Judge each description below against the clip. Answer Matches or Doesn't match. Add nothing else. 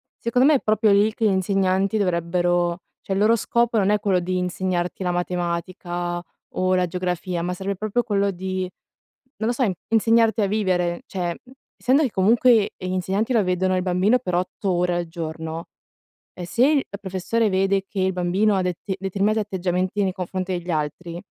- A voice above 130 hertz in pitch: Matches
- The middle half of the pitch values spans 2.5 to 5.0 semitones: Matches